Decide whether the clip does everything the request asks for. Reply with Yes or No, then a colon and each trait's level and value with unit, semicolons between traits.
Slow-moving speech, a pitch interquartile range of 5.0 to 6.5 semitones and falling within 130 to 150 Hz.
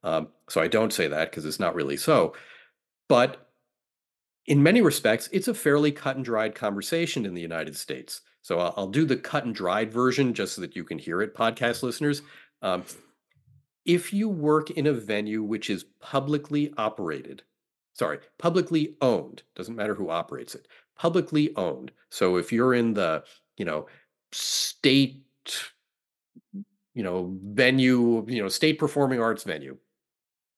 No: average, 160 wpm; wide, 5.4 semitones; low, 135 Hz